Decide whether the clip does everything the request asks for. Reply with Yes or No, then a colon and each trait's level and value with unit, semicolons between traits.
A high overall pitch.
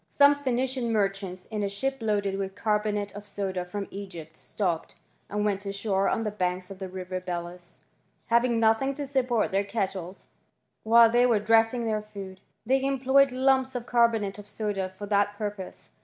Yes: high, 210 Hz